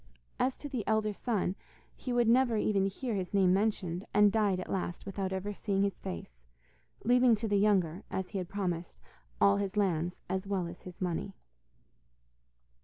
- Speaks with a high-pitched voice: Yes, high, 200 Hz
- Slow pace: No, average, 180 wpm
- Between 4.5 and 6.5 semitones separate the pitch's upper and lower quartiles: No, average, 2.7 semitones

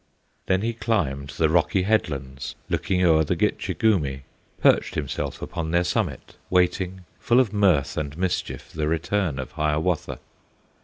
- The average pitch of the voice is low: Yes, very low, 85 Hz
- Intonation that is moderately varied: Yes, average, 4.2 semitones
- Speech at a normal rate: Yes, average, 145 wpm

